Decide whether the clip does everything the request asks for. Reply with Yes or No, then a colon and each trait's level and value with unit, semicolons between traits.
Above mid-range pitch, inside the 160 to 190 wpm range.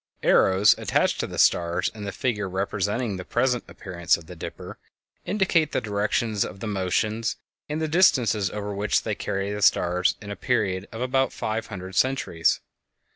No: low, 105 Hz; average, 180 wpm